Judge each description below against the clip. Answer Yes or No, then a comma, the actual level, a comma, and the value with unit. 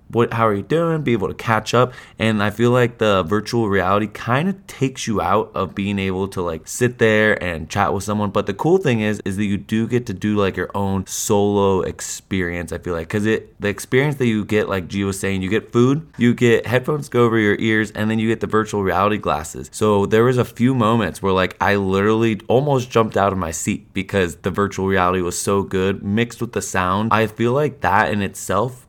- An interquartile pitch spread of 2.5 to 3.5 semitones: Yes, average, 3.2 semitones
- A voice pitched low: Yes, low, 105 Hz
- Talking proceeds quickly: Yes, fast, 240 wpm